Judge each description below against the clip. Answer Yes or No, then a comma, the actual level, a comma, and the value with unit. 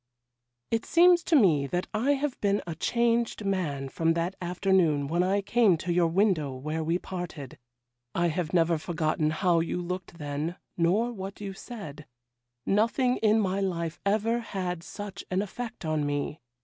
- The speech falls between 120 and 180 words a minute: Yes, average, 165 wpm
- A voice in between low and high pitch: Yes, medium, 180 Hz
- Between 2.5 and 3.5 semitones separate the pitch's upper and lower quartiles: No, average, 4.2 semitones